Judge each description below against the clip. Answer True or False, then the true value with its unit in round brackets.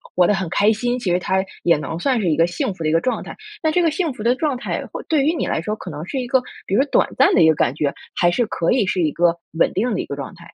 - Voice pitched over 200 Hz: False (195 Hz)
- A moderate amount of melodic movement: False (7.0 semitones)